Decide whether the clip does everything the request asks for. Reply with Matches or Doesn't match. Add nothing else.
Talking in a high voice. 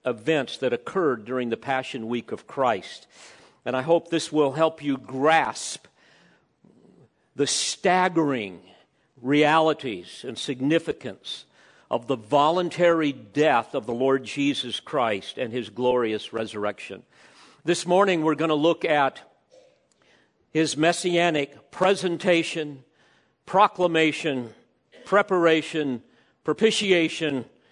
Doesn't match